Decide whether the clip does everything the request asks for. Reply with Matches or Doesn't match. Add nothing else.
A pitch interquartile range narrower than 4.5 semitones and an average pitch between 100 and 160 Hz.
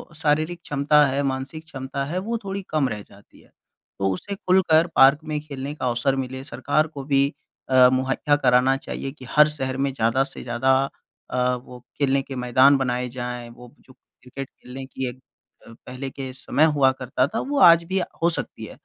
Matches